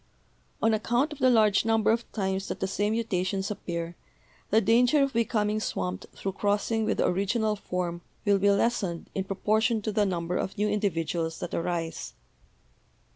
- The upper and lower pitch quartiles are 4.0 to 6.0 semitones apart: No, average, 3.5 semitones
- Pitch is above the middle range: Yes, high, 205 Hz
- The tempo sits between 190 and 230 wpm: No, average, 170 wpm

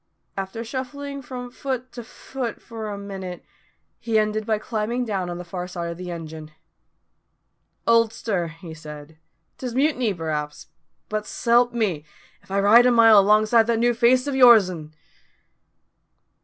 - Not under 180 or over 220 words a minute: No, average, 150 wpm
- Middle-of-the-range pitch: No, high, 215 Hz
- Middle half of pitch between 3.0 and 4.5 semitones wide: No, average, 5.1 semitones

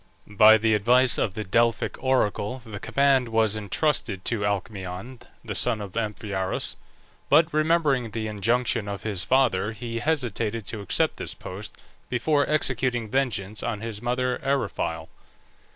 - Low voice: Yes, low, 115 Hz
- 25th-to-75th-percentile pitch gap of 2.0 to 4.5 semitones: Yes, average, 3.8 semitones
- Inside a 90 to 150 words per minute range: Yes, average, 140 wpm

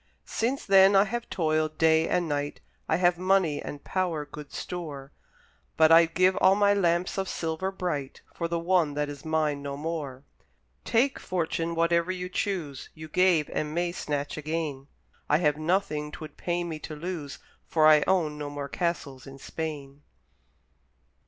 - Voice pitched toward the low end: No, medium, 160 Hz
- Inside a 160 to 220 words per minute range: Yes, average, 165 wpm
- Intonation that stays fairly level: No, average, 3.4 semitones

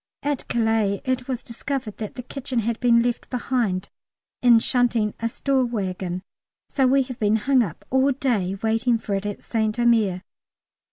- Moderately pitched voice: No, high, 235 Hz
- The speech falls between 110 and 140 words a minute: No, average, 170 wpm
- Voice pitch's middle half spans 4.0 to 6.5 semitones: No, average, 3.1 semitones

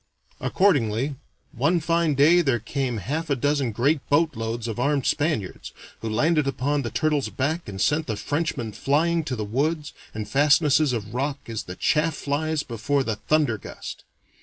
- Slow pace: No, average, 165 wpm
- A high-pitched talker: No, medium, 140 Hz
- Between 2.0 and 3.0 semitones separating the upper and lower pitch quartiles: No, average, 4.8 semitones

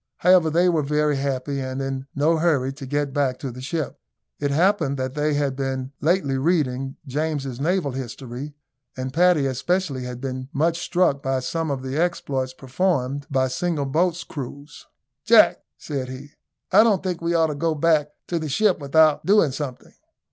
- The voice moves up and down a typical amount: Yes, average, 3.7 semitones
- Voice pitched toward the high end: No, medium, 145 Hz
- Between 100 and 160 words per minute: No, average, 175 wpm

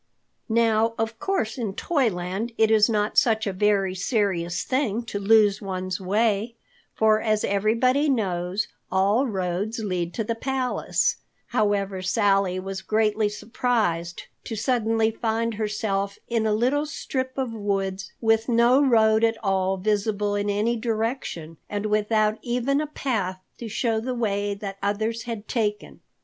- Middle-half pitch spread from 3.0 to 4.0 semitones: No, narrow, 2.6 semitones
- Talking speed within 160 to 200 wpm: No, average, 145 wpm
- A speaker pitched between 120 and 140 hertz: No, high, 215 Hz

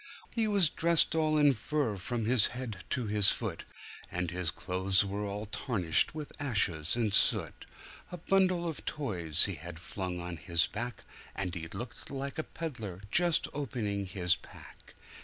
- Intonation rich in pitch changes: Yes, wide, 8.0 semitones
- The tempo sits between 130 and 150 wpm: No, average, 165 wpm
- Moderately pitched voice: No, low, 105 Hz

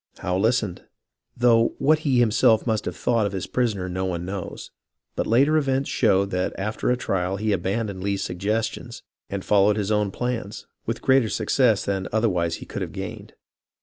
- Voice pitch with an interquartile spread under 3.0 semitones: No, average, 3.6 semitones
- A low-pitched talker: Yes, low, 105 Hz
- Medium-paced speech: Yes, average, 180 wpm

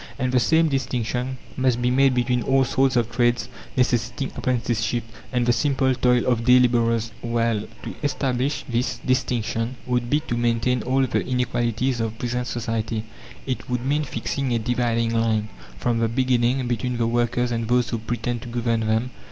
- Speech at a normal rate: Yes, average, 175 wpm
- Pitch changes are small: Yes, narrow, 1.6 semitones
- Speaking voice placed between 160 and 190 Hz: No, low, 120 Hz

